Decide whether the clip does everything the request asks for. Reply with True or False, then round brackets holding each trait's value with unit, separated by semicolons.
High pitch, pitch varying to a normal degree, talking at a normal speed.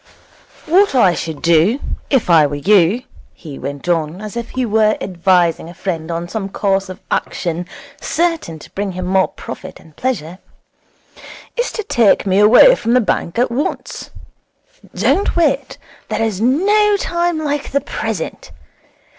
False (205 Hz; 7.6 semitones; 155 wpm)